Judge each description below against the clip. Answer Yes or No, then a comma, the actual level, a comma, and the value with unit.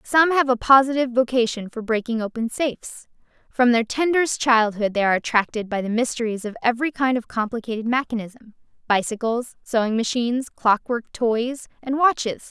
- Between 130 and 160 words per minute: Yes, average, 155 wpm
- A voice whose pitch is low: No, high, 240 Hz